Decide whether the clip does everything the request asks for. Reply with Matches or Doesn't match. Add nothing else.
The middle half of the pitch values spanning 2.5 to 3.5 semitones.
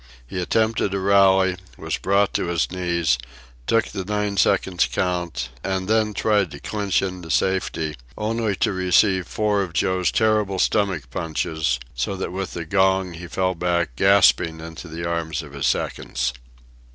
Matches